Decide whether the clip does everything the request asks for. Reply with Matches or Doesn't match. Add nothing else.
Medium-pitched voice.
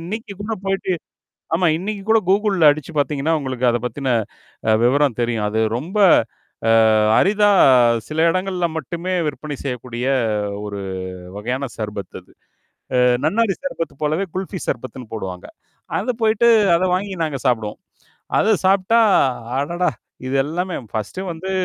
Matches